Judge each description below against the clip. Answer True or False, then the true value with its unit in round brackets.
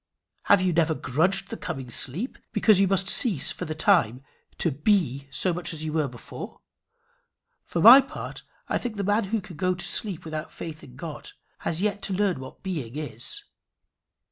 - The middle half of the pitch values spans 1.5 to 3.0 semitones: False (4.8 semitones)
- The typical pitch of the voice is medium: True (175 Hz)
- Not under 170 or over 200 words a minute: True (190 wpm)